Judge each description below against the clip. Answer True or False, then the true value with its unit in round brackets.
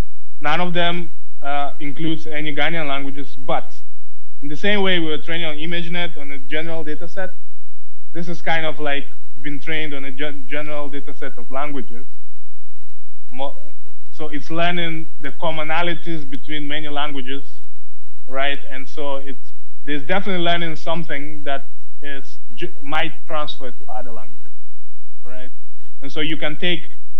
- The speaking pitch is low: False (150 Hz)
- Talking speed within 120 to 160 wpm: True (150 wpm)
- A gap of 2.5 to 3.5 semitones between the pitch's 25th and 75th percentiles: True (2.8 semitones)